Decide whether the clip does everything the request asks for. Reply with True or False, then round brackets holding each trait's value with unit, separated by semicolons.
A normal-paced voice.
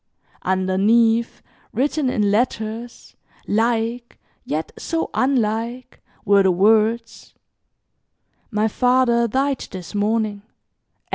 False (85 wpm)